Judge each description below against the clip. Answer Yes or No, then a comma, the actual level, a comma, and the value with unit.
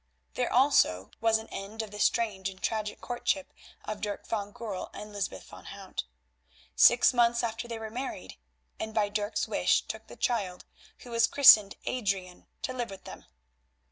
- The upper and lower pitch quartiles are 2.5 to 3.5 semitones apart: Yes, average, 2.8 semitones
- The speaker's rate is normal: Yes, average, 170 wpm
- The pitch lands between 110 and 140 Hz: No, high, 220 Hz